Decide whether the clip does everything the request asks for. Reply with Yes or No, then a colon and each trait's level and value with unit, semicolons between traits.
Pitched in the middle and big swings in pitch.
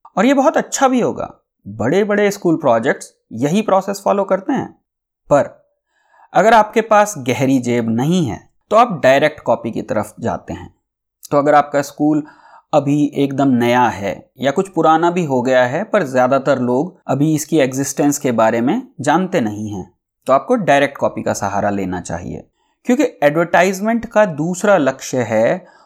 Yes: medium, 150 Hz; wide, 7.6 semitones